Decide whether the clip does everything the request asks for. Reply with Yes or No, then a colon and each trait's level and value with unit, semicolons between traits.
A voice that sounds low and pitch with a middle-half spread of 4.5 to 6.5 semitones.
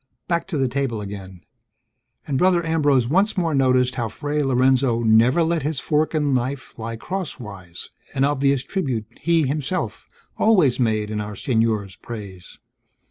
Yes: low, 130 Hz; average, 5.3 semitones